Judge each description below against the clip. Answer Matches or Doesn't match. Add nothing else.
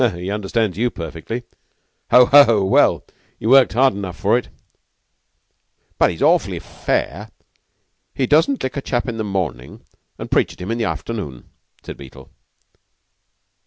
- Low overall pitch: Matches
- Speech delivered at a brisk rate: Doesn't match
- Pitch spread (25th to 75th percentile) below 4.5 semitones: Doesn't match